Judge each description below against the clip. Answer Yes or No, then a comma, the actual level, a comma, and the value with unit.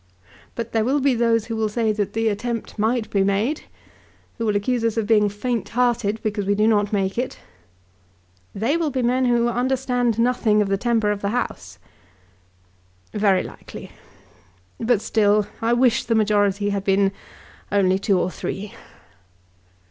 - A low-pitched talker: No, high, 220 Hz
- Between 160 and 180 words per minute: Yes, average, 165 wpm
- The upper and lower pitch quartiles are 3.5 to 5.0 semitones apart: No, average, 2.8 semitones